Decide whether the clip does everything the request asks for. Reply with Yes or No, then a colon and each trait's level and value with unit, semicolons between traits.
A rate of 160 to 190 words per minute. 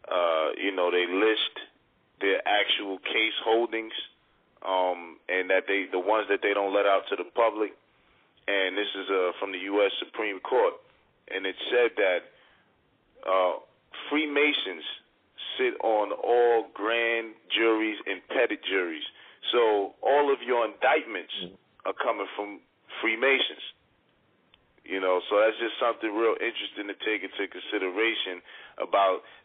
No: average, 140 wpm